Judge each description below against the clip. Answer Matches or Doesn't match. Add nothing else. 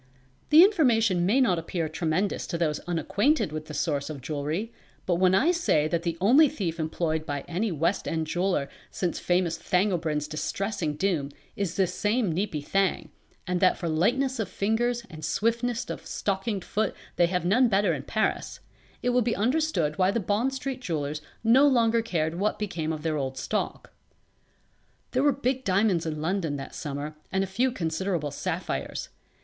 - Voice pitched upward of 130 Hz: Matches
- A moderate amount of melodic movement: Doesn't match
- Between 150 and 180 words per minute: Matches